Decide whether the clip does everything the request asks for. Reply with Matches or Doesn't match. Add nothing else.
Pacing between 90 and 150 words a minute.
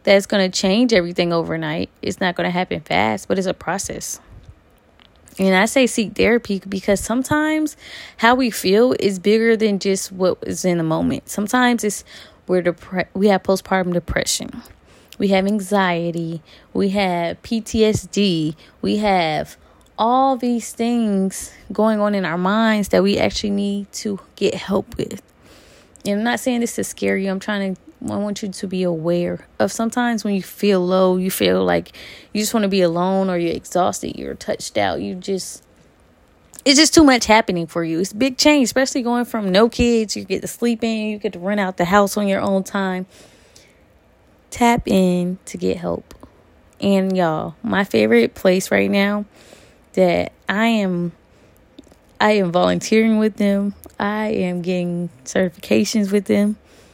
Doesn't match